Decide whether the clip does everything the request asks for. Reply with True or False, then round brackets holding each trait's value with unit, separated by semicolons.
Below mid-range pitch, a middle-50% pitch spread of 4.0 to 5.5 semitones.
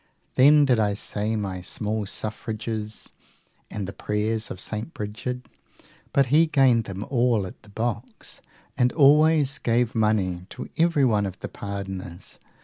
False (110 Hz; 3.6 semitones)